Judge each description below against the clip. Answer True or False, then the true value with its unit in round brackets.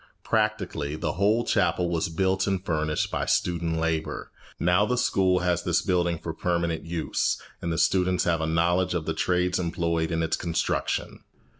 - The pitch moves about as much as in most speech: False (1.8 semitones)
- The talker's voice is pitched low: True (85 Hz)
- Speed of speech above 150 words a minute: True (170 wpm)